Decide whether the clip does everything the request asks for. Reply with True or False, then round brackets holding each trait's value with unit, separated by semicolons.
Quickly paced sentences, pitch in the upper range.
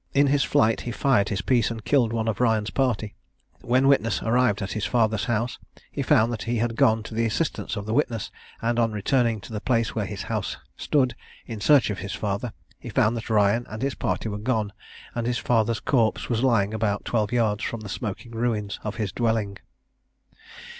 False (210 wpm; 115 Hz)